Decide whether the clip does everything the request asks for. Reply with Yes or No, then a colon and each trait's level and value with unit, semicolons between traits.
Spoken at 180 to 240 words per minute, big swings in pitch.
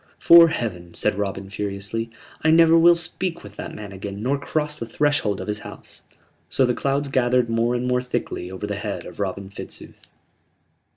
Yes: average, 185 wpm; wide, 6.2 semitones